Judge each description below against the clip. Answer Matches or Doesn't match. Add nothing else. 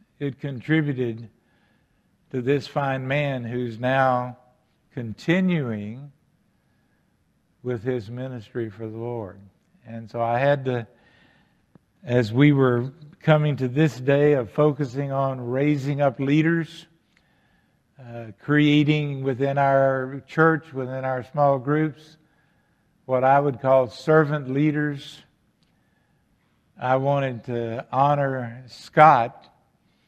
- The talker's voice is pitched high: Doesn't match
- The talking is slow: Matches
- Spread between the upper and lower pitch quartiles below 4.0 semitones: Matches